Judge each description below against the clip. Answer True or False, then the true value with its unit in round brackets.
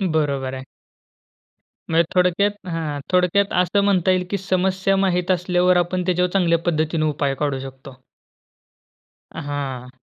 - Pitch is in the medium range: True (175 Hz)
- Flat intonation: False (4.1 semitones)